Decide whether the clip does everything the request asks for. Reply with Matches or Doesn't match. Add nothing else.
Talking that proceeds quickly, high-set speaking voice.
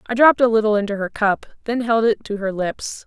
Matches